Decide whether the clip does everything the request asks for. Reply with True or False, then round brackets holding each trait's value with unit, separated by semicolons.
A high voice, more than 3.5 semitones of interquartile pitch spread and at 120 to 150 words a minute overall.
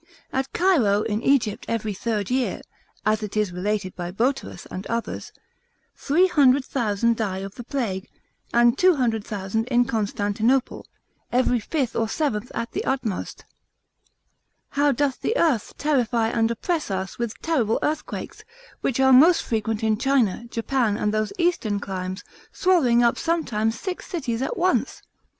True (235 Hz; 4.3 semitones; 140 wpm)